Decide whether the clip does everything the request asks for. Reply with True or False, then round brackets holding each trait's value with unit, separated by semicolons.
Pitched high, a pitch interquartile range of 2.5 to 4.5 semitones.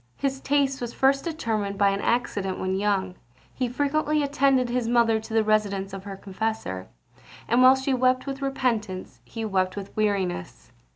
False (225 Hz; 5.1 semitones)